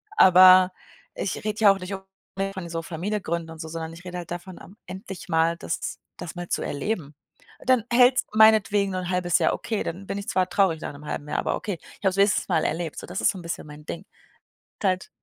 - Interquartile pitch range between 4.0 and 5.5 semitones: No, average, 2.9 semitones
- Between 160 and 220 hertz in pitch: Yes, medium, 185 Hz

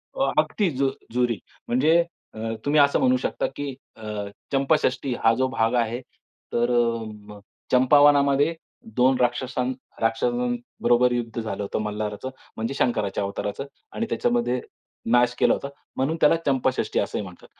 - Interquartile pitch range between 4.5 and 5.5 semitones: No, average, 3.4 semitones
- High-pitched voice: No, low, 125 Hz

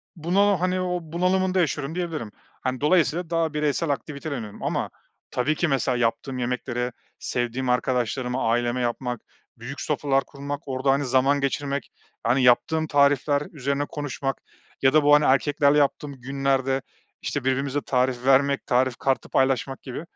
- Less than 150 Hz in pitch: Yes, medium, 140 Hz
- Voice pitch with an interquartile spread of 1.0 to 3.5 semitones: Yes, average, 2.8 semitones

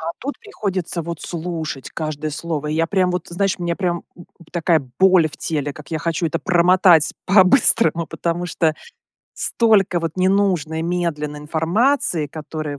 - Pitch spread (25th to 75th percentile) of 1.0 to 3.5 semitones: Yes, average, 2.8 semitones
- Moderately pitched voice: Yes, medium, 170 Hz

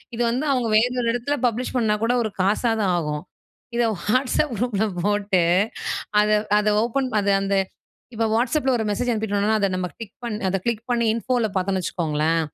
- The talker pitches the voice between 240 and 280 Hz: No, high, 220 Hz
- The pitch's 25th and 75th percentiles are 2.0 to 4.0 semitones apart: Yes, average, 3.4 semitones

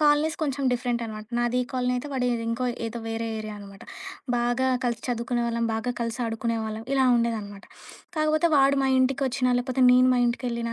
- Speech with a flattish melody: Yes, narrow, 2.1 semitones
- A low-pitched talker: No, high, 240 Hz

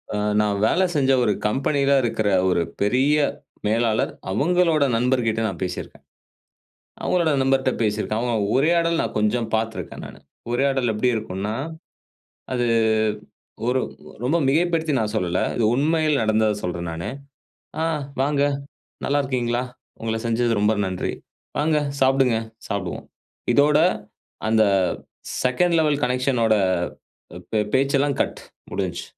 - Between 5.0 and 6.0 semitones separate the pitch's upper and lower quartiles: No, average, 4.5 semitones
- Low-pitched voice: Yes, low, 125 Hz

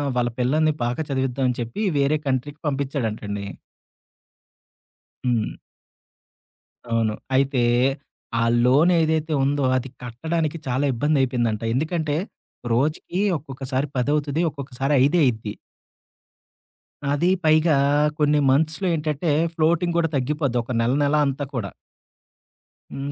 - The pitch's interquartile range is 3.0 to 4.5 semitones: Yes, average, 3.7 semitones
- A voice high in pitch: No, medium, 140 Hz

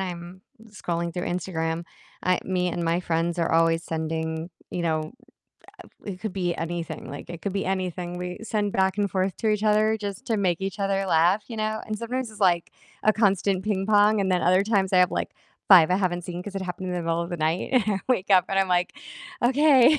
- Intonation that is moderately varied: Yes, average, 3.1 semitones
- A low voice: No, medium, 185 Hz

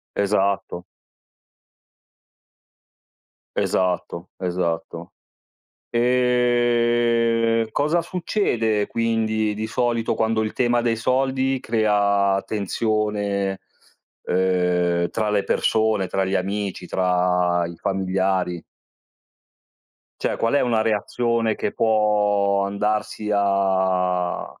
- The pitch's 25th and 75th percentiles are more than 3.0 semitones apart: Yes, average, 3.4 semitones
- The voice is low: Yes, low, 105 Hz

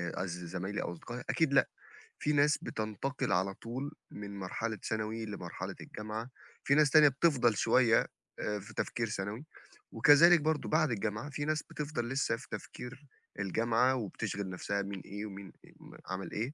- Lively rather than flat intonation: Yes, wide, 5.7 semitones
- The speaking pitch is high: No, low, 115 Hz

